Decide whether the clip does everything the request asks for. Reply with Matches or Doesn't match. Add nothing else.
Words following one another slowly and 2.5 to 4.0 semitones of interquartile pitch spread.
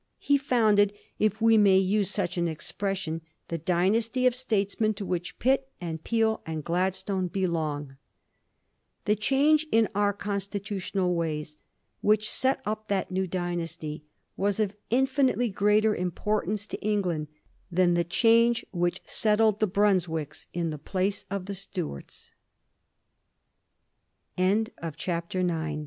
Matches